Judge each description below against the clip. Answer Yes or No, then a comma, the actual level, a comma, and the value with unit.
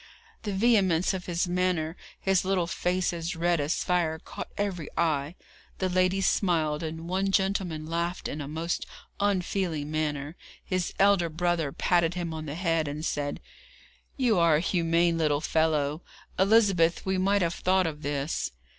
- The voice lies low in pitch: No, medium, 170 Hz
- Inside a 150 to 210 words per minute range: Yes, average, 160 wpm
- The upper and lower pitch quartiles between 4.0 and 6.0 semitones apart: No, average, 2.9 semitones